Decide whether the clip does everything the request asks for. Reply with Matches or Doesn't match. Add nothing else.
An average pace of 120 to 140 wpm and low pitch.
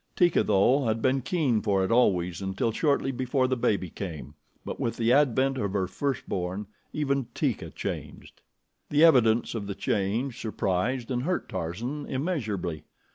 Doesn't match